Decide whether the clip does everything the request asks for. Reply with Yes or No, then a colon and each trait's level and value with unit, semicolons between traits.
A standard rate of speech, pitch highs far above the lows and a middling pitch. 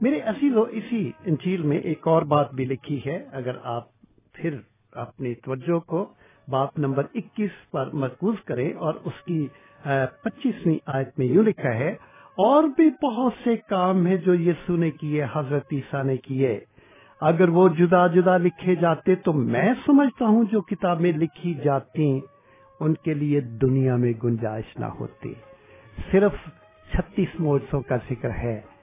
Yes: average, 155 wpm; wide, 5.7 semitones; medium, 160 Hz